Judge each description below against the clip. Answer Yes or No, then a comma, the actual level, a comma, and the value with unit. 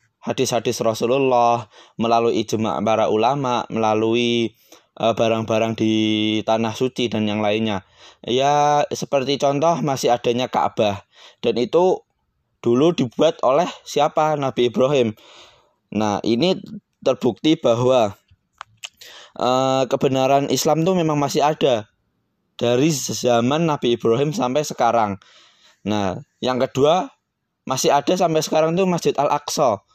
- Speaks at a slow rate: No, average, 110 wpm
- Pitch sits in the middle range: No, low, 125 Hz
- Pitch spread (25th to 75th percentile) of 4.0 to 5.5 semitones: Yes, average, 4.3 semitones